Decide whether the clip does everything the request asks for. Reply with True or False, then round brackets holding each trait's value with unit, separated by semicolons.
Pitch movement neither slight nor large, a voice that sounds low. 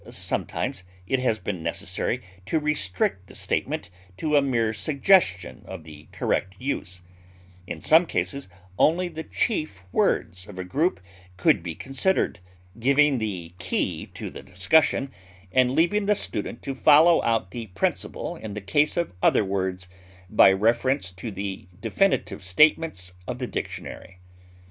False (8.1 semitones; 115 Hz)